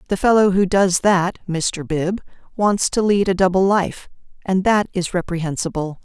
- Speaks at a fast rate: No, average, 170 wpm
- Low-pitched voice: No, medium, 185 Hz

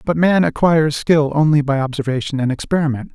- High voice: No, medium, 150 Hz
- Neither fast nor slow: Yes, average, 170 wpm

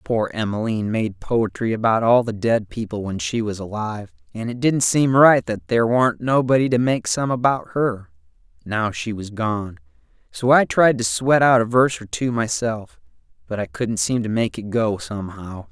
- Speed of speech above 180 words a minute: Yes, average, 195 wpm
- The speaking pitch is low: Yes, low, 110 Hz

